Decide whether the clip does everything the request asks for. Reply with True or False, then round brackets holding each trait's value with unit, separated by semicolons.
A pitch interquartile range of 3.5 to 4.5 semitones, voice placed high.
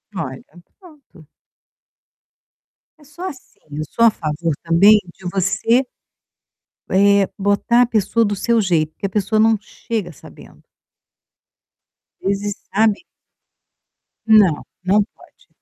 True (3.8 semitones; 205 Hz)